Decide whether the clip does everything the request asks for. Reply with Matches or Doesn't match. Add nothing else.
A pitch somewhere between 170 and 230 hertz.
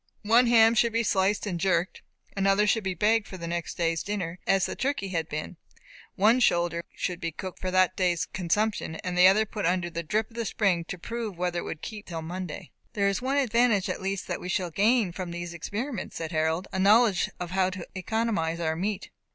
Matches